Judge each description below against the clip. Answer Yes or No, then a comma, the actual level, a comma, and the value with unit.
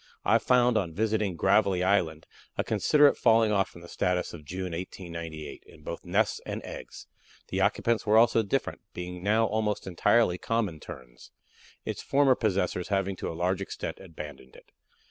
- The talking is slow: No, average, 165 wpm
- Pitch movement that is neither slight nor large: Yes, average, 4.2 semitones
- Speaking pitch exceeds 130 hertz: No, very low, 95 Hz